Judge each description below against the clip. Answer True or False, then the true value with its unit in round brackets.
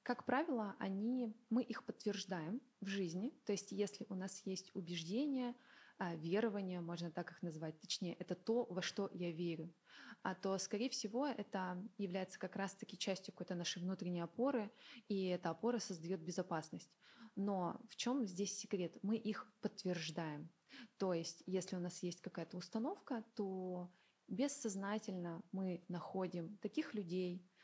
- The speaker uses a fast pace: False (145 wpm)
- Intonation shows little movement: False (3.8 semitones)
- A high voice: True (195 Hz)